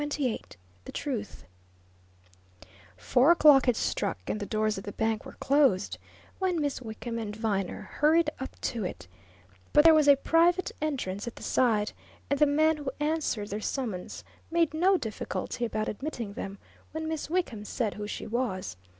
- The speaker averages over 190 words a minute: No, average, 170 wpm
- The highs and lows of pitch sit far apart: Yes, wide, 6.2 semitones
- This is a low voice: No, very high, 255 Hz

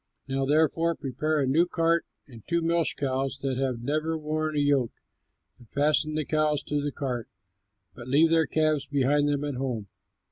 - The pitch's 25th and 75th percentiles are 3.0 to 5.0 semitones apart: No, narrow, 2.6 semitones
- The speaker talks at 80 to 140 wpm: No, average, 180 wpm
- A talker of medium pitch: Yes, medium, 145 Hz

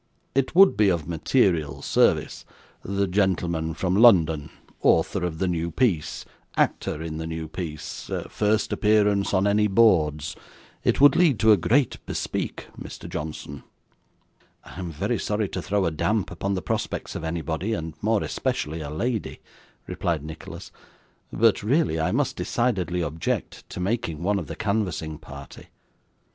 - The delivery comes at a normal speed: Yes, average, 155 wpm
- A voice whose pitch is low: Yes, very low, 90 Hz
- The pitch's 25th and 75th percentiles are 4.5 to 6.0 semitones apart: Yes, average, 4.8 semitones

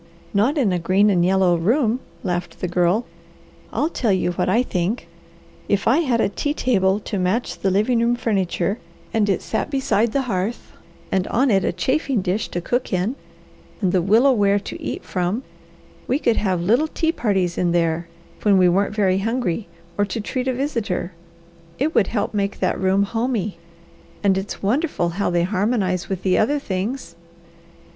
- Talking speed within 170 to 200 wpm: Yes, average, 180 wpm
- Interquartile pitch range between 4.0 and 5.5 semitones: Yes, average, 4.6 semitones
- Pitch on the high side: Yes, high, 200 Hz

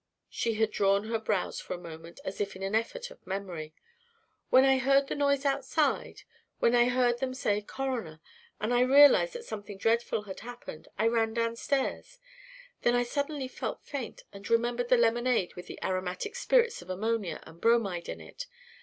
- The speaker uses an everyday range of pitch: Yes, average, 4.9 semitones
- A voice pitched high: Yes, high, 230 Hz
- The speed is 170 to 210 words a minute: Yes, average, 180 wpm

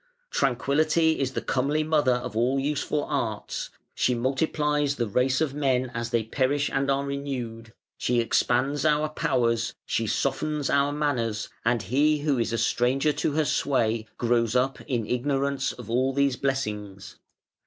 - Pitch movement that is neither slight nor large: Yes, average, 3.4 semitones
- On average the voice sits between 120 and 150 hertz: Yes, low, 135 Hz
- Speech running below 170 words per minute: Yes, average, 155 wpm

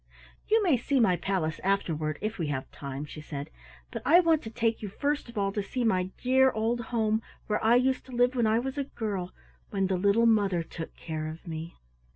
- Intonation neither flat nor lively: No, wide, 5.8 semitones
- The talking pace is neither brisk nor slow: No, fast, 220 wpm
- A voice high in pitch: Yes, high, 215 Hz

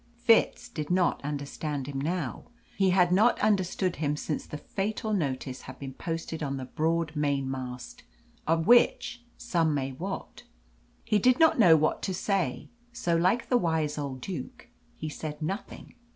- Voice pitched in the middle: Yes, medium, 165 Hz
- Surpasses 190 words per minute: No, average, 160 wpm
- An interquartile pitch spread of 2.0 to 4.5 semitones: No, average, 5.0 semitones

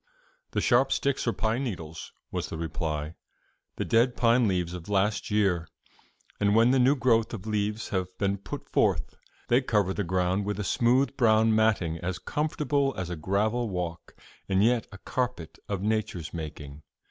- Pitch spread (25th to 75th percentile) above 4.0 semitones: Yes, average, 4.7 semitones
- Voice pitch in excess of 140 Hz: No, low, 105 Hz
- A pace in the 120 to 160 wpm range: No, average, 170 wpm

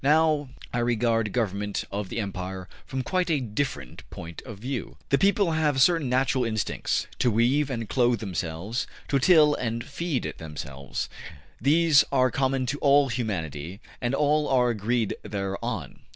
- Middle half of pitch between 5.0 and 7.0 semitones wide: Yes, average, 5.3 semitones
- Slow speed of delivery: No, average, 150 wpm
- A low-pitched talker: Yes, low, 120 Hz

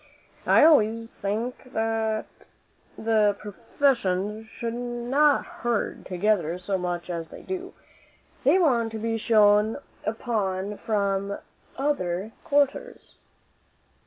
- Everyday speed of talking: No, slow, 100 wpm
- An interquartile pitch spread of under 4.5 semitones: Yes, average, 3.2 semitones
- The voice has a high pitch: Yes, high, 220 Hz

